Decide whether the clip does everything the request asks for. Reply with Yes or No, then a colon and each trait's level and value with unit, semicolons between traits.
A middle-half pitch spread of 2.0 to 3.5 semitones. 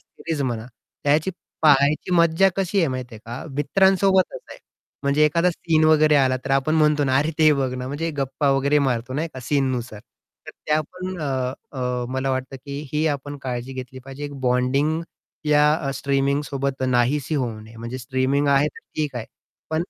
Yes: average, 2.8 semitones